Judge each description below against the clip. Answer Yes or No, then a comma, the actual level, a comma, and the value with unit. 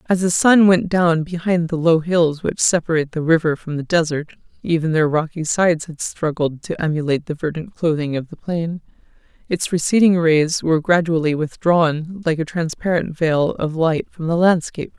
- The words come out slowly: No, average, 170 wpm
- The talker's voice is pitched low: No, medium, 165 Hz